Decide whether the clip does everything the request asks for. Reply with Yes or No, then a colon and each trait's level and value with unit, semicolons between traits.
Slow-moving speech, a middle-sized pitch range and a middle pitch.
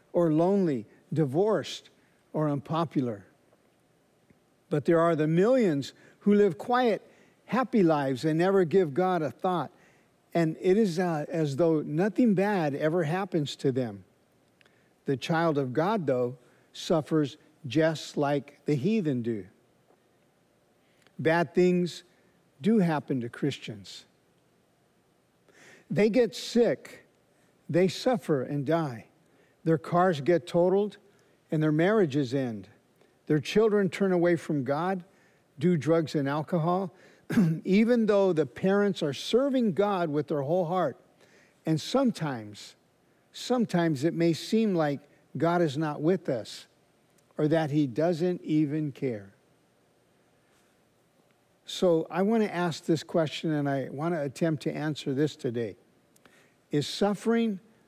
Yes: slow, 125 wpm; average, 4.1 semitones; medium, 165 Hz